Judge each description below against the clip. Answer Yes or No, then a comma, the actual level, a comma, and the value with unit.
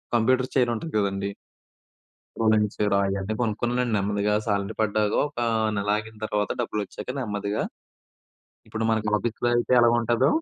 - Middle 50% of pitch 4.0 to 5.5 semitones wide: No, narrow, 2.5 semitones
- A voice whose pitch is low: Yes, low, 110 Hz